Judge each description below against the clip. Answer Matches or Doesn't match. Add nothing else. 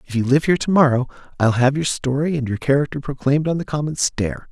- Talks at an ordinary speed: Doesn't match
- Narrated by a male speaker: Matches